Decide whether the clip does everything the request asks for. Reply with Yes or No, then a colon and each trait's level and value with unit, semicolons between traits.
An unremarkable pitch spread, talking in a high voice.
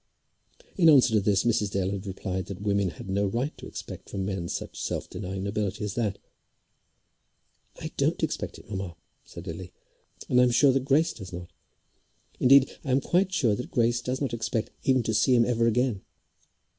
No: average, 4.5 semitones; low, 110 Hz